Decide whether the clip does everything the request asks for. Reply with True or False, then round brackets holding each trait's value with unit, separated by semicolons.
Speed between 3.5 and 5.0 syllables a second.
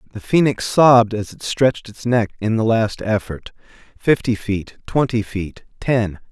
True (4.5 syllables/s)